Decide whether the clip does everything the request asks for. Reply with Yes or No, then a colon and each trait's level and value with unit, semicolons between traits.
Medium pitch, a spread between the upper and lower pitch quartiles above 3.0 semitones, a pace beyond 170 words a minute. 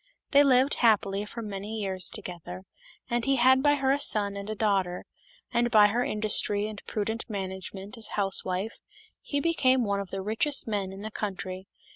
No: high, 210 Hz; average, 3.6 semitones; average, 185 wpm